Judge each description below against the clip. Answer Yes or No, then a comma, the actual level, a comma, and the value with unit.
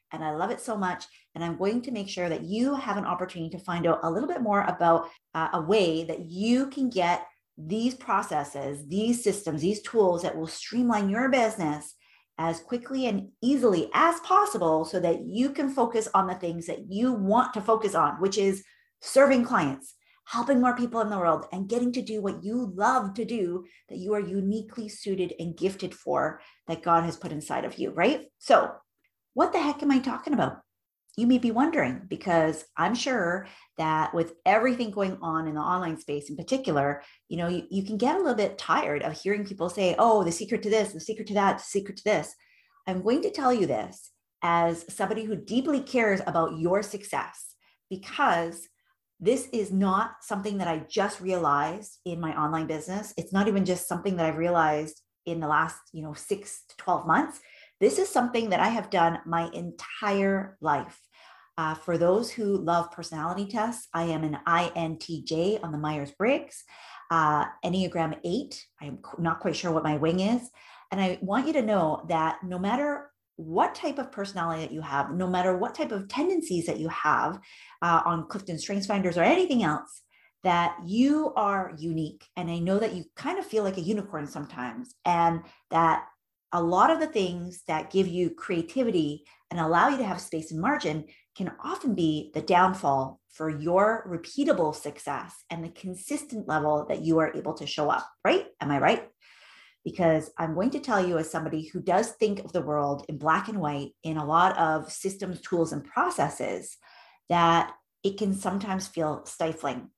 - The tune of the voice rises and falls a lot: No, average, 4.9 semitones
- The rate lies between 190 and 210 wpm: Yes, average, 195 wpm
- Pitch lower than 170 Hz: No, medium, 185 Hz